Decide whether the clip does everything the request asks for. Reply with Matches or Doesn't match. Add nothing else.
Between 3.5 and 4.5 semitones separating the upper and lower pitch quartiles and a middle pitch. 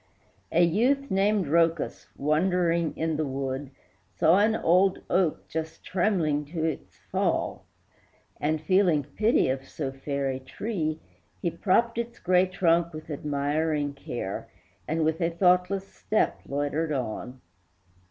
Matches